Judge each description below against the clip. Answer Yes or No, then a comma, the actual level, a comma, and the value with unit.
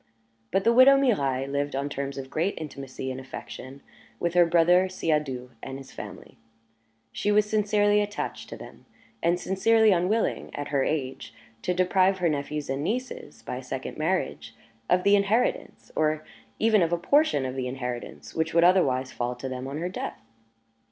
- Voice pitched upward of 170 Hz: No, medium, 165 Hz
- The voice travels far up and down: Yes, wide, 6.6 semitones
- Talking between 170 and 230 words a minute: Yes, average, 175 wpm